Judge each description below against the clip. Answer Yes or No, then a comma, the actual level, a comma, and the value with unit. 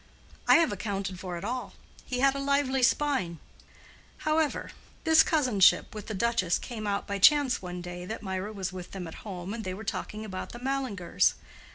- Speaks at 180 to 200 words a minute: Yes, average, 185 wpm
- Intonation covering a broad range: Yes, wide, 6.1 semitones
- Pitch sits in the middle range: No, high, 215 Hz